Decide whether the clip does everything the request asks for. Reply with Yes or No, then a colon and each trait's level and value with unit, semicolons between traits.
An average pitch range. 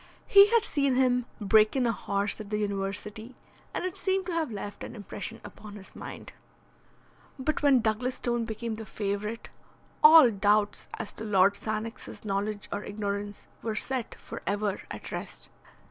Yes: average, 3.6 semitones